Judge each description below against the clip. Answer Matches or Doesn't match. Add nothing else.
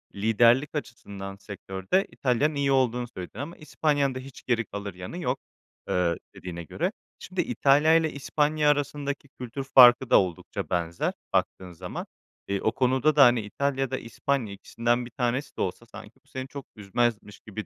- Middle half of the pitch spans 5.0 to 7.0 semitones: Matches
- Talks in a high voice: Doesn't match